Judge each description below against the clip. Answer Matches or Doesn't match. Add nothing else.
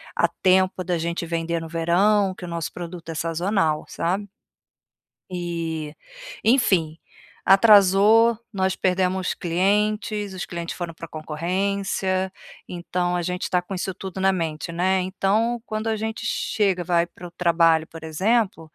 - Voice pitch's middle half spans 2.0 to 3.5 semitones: Matches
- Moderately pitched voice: Matches